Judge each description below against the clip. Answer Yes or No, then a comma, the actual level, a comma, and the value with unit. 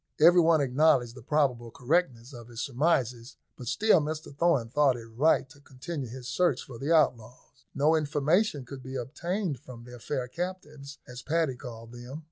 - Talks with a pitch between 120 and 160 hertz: Yes, low, 135 Hz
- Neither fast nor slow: Yes, average, 175 wpm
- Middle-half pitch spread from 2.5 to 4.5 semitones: Yes, average, 4.2 semitones